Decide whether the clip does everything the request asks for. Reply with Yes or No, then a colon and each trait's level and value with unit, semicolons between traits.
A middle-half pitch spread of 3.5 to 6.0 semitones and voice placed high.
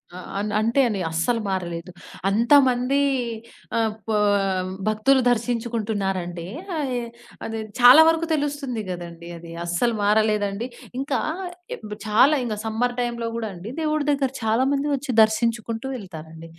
Yes: average, 4.0 semitones; high, 225 Hz